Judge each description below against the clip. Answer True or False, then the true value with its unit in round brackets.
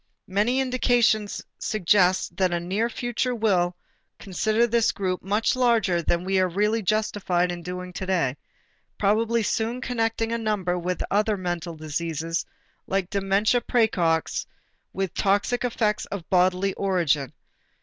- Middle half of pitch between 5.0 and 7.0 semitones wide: False (3.8 semitones)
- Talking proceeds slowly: True (130 wpm)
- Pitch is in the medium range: False (195 Hz)